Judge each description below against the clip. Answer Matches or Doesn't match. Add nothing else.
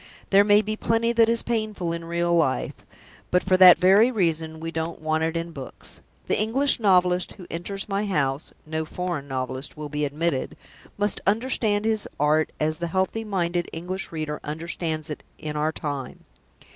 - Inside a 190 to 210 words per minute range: Doesn't match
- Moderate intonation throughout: Matches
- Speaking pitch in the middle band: Matches